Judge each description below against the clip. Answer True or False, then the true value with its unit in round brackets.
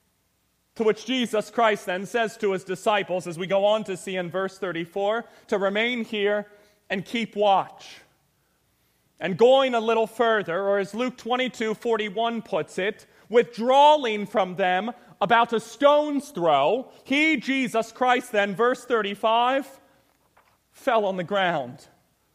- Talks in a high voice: True (215 Hz)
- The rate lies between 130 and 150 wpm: True (140 wpm)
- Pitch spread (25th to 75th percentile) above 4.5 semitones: False (3.3 semitones)